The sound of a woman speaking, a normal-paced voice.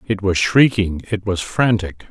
No: male; average, 170 wpm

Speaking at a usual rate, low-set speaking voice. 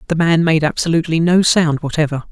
No: average, 180 wpm; medium, 160 Hz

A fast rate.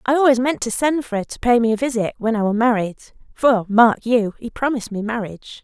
Yes: fast, 245 wpm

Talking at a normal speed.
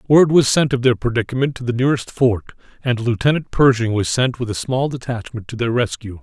No: fast, 210 wpm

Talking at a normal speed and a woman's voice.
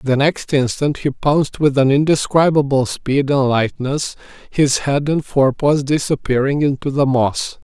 No: average, 150 wpm; male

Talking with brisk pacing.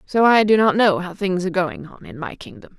Yes: fast, 280 wpm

